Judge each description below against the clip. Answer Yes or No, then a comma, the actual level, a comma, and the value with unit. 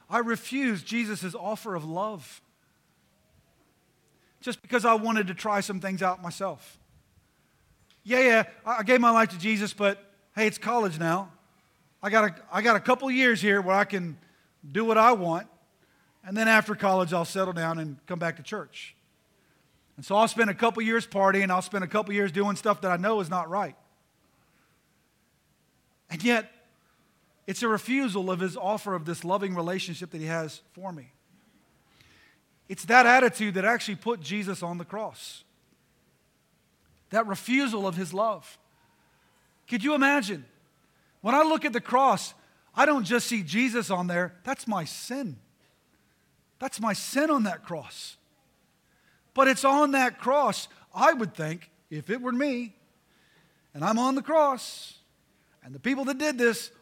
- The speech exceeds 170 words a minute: No, average, 165 wpm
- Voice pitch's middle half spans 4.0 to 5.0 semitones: Yes, average, 4.6 semitones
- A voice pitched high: Yes, high, 205 Hz